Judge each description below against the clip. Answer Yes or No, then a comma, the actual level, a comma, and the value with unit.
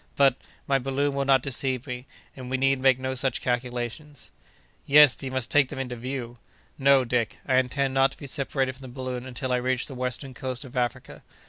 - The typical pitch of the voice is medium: No, low, 130 Hz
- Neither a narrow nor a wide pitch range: No, narrow, 1.4 semitones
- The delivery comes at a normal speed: No, fast, 215 wpm